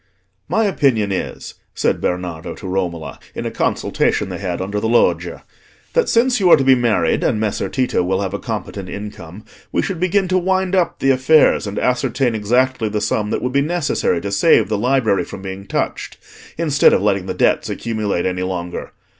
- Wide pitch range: Yes, wide, 6.5 semitones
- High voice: No, low, 110 Hz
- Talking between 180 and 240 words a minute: Yes, average, 195 wpm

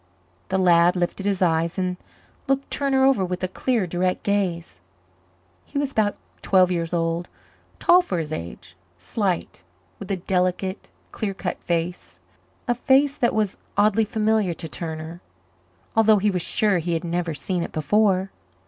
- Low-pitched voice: No, medium, 185 Hz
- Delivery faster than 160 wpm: No, average, 155 wpm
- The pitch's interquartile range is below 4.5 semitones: Yes, average, 3.8 semitones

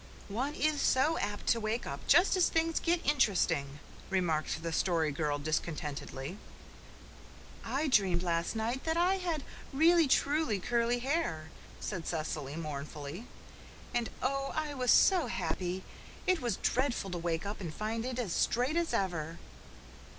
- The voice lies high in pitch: Yes, high, 220 Hz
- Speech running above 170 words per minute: No, average, 150 wpm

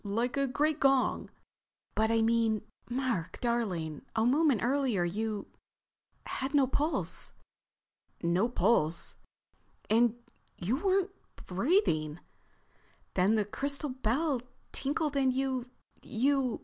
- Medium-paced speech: No, slow, 90 wpm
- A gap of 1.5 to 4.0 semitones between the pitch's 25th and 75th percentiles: No, average, 4.4 semitones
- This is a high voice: Yes, high, 245 Hz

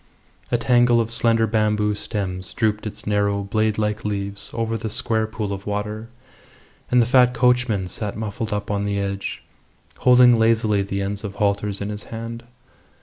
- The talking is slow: No, average, 170 wpm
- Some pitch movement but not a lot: No, narrow, 2.2 semitones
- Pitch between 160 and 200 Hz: No, low, 105 Hz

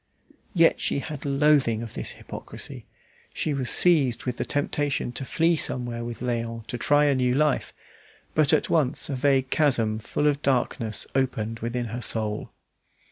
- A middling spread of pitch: Yes, average, 3.8 semitones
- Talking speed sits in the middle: Yes, average, 165 wpm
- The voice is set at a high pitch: No, low, 130 Hz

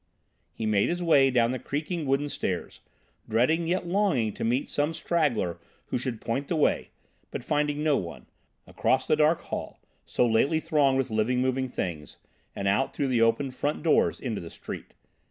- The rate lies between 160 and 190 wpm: Yes, average, 180 wpm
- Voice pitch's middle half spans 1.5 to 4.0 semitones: No, average, 4.9 semitones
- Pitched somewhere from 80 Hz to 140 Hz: Yes, low, 135 Hz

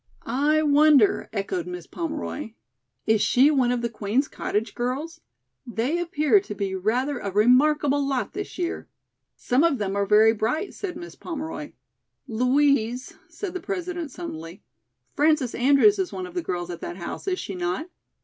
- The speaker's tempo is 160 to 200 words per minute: Yes, average, 165 wpm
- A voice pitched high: Yes, very high, 275 Hz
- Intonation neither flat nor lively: No, wide, 6.9 semitones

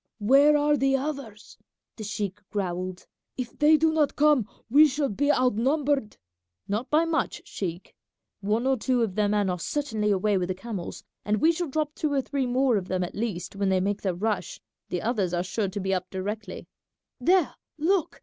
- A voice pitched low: No, high, 225 Hz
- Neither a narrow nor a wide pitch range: No, wide, 6.5 semitones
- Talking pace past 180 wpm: Yes, average, 195 wpm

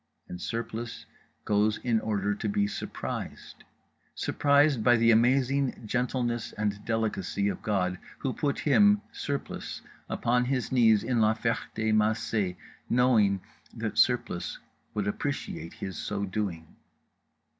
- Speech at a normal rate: No, slow, 120 wpm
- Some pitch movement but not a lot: Yes, average, 3.3 semitones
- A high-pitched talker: No, low, 110 Hz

